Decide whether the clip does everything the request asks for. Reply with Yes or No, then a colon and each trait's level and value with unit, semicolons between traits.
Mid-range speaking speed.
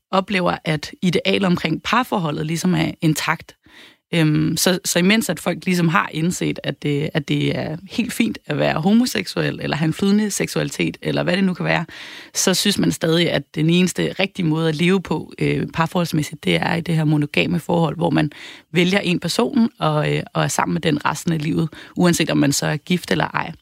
Yes: average, 190 wpm